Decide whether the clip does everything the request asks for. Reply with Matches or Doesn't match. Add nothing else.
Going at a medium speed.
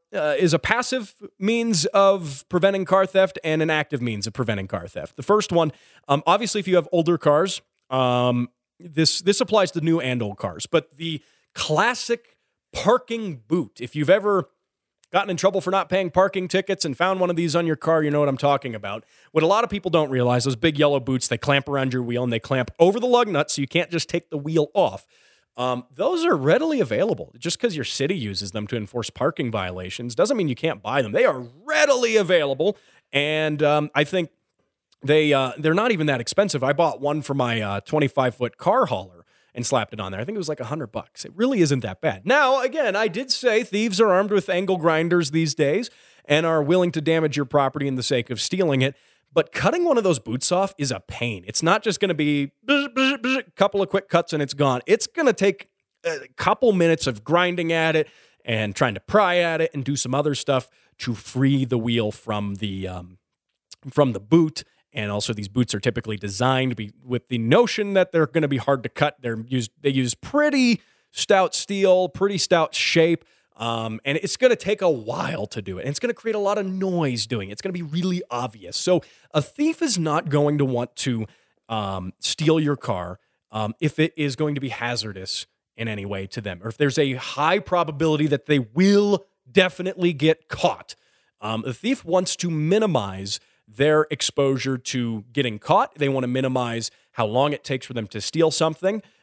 Doesn't match